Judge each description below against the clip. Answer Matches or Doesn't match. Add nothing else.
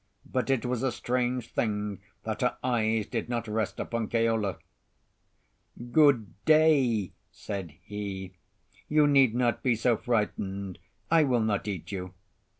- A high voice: Doesn't match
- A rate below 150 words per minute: Matches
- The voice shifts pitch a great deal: Doesn't match